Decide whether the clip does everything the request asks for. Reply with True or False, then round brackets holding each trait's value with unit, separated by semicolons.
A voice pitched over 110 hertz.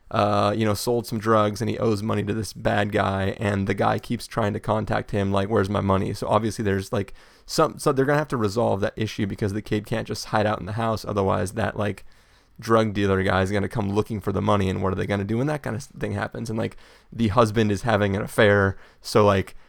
False (105 Hz)